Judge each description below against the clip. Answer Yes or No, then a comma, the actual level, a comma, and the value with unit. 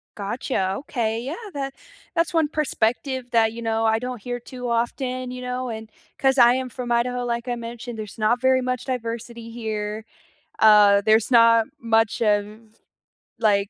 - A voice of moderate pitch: No, high, 235 Hz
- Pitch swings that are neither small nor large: No, narrow, 2.2 semitones